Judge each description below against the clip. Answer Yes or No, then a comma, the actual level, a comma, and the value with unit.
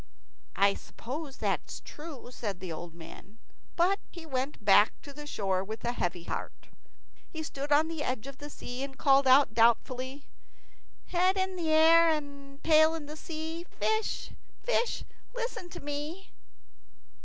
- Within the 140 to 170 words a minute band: Yes, average, 155 wpm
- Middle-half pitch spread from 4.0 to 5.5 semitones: Yes, average, 4.9 semitones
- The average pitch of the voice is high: Yes, very high, 285 Hz